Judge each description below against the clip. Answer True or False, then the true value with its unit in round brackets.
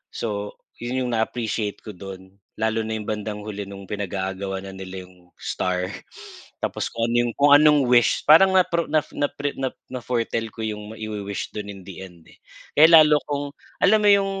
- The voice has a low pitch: True (110 Hz)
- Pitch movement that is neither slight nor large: False (6.2 semitones)